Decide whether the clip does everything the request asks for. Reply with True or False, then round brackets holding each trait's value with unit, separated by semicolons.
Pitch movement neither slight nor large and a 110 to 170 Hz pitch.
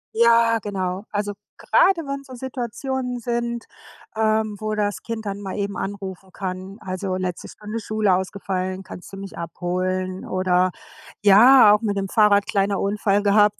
False (3.0 semitones; 205 Hz)